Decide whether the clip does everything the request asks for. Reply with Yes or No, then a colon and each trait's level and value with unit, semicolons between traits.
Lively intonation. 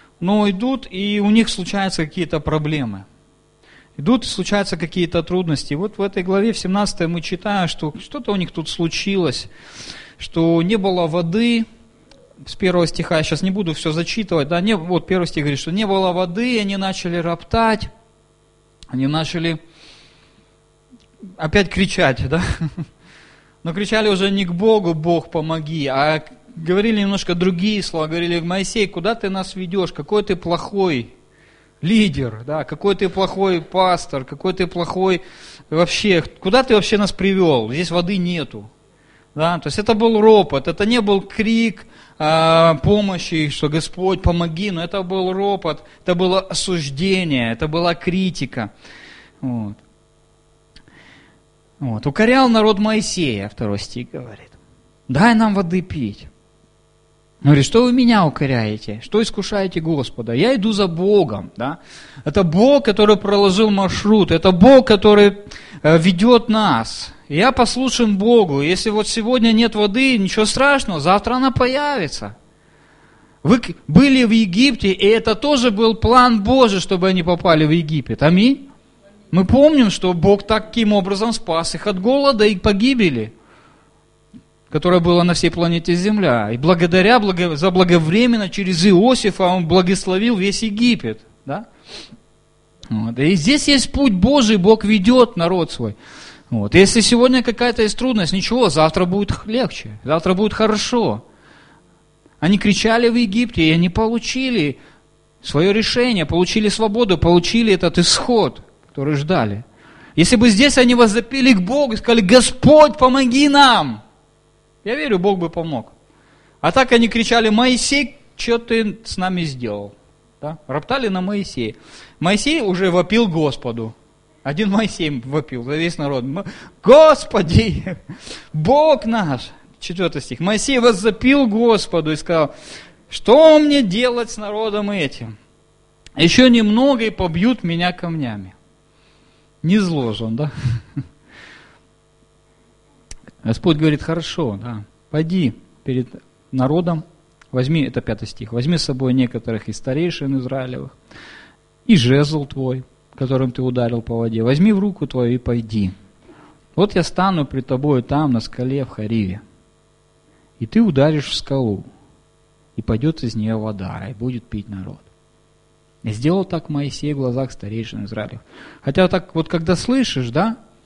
Yes: wide, 6.1 semitones